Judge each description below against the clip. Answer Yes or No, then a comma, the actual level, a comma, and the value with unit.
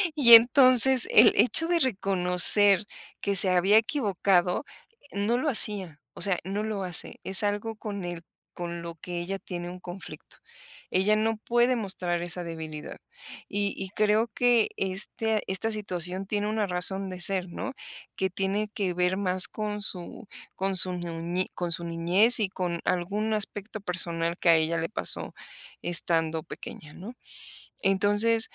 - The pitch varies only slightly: No, average, 3.3 semitones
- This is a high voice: Yes, high, 195 Hz